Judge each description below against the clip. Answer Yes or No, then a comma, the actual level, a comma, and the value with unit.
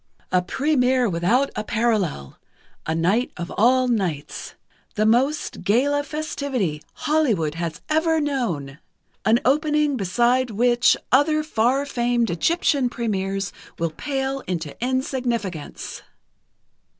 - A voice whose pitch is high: Yes, high, 240 Hz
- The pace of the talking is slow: Yes, slow, 110 wpm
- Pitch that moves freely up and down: Yes, wide, 6.4 semitones